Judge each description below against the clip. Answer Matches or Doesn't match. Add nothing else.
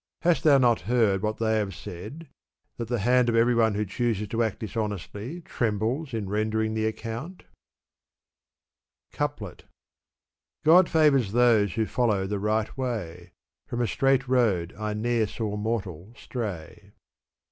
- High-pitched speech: Doesn't match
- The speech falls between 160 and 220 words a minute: Doesn't match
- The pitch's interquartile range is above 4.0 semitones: Doesn't match